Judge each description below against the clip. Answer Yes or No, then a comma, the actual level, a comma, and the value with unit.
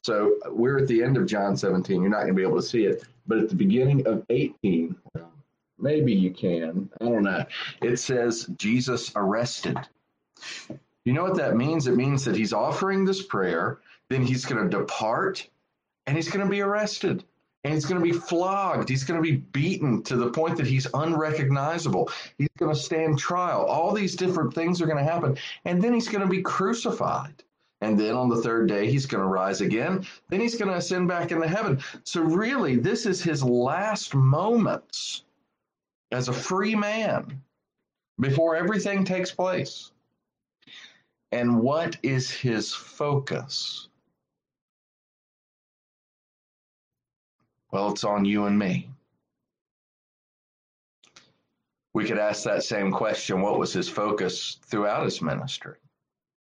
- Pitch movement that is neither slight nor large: No, wide, 6.9 semitones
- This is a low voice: No, medium, 150 Hz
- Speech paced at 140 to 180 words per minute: Yes, average, 160 wpm